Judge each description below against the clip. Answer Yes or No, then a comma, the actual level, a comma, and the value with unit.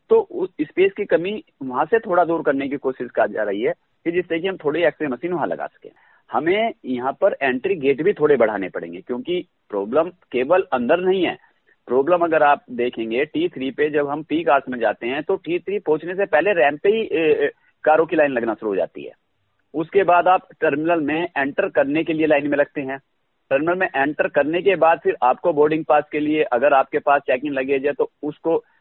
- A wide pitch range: Yes, wide, 5.7 semitones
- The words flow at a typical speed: No, fast, 220 wpm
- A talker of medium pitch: Yes, medium, 160 Hz